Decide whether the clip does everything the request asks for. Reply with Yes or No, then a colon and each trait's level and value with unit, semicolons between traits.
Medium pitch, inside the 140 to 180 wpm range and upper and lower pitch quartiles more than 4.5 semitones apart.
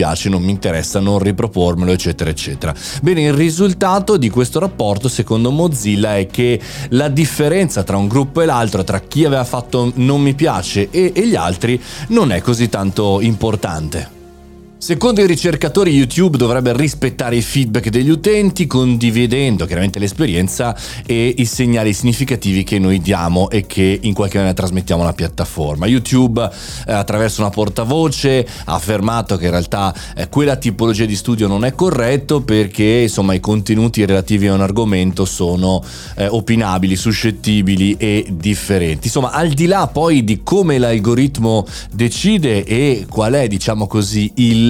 No: low, 115 Hz; average, 150 wpm; average, 5.1 semitones